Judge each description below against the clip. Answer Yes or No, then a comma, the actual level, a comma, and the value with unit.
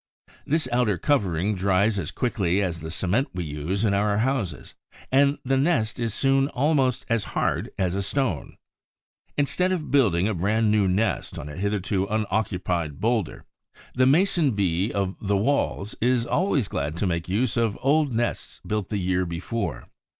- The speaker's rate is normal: Yes, average, 165 wpm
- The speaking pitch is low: Yes, low, 105 Hz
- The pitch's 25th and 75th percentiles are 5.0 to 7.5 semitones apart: Yes, wide, 5.6 semitones